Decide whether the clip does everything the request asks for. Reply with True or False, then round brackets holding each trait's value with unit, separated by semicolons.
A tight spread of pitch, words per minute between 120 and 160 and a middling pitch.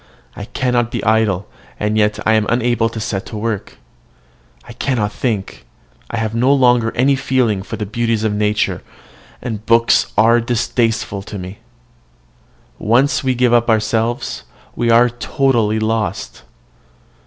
False (2.2 semitones; 145 wpm; 115 Hz)